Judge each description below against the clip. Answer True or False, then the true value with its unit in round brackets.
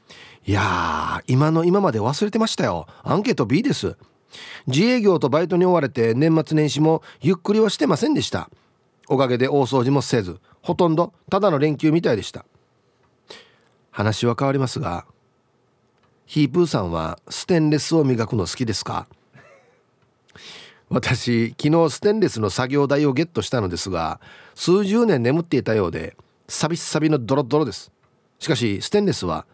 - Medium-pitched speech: True (145 Hz)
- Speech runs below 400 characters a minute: True (330 characters per minute)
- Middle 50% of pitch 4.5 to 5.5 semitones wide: True (5.2 semitones)